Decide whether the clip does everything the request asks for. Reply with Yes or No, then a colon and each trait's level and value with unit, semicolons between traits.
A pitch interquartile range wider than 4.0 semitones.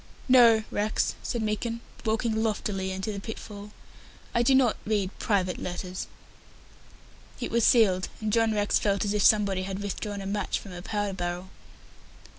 No: narrow, 2.4 semitones